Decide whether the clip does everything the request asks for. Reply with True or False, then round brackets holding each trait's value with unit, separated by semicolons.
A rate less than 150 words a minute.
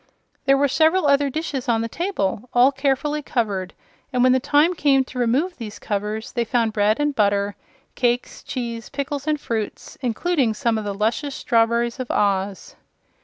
False (170 wpm)